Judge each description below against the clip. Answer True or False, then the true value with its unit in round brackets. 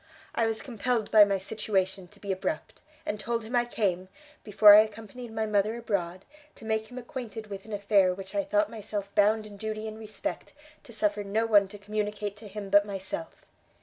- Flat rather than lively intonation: True (1.9 semitones)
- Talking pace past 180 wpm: True (200 wpm)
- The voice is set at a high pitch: True (210 Hz)